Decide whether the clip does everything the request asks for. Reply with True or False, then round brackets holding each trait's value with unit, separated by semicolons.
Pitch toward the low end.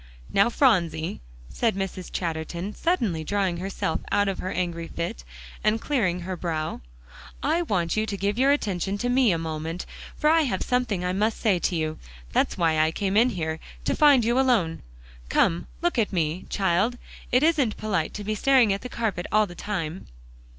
False (195 Hz)